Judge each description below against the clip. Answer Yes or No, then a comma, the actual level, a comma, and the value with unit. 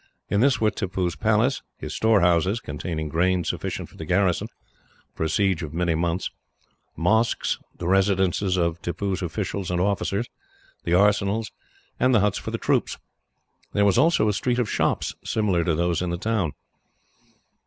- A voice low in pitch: Yes, very low, 95 Hz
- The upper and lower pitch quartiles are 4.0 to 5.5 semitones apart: No, average, 3.5 semitones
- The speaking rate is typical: Yes, average, 165 wpm